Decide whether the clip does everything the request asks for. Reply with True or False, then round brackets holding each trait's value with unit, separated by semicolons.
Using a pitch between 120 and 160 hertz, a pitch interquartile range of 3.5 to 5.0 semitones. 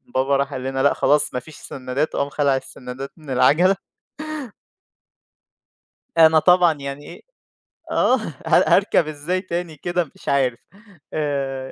False (140 Hz; 3.1 semitones)